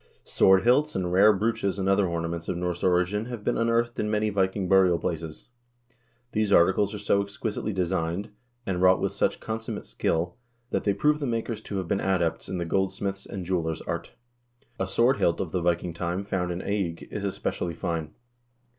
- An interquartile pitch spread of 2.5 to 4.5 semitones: Yes, average, 3.0 semitones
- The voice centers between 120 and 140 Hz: No, very low, 95 Hz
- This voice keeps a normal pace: Yes, average, 190 wpm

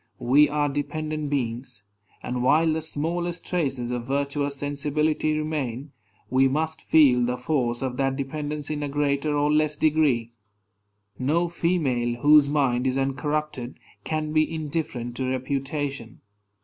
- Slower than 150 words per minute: Yes, slow, 135 wpm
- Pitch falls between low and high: Yes, medium, 145 Hz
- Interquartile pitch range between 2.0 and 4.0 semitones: Yes, average, 2.8 semitones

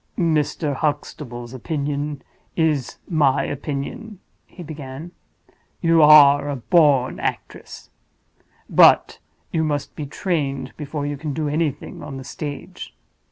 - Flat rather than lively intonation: Yes, narrow, 2.3 semitones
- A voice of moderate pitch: Yes, medium, 145 Hz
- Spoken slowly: Yes, slow, 115 wpm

